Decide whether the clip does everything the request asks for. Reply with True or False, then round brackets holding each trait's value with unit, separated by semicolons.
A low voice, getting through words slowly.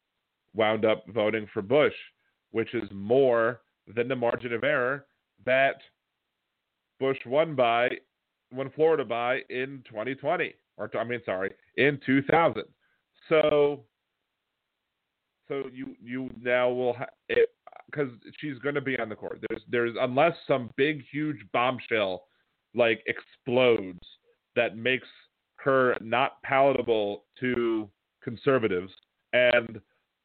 True (125 Hz; 120 wpm)